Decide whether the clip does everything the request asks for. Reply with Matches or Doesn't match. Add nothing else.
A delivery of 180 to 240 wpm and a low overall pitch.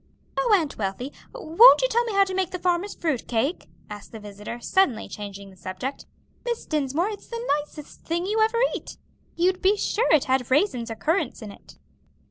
Doesn't match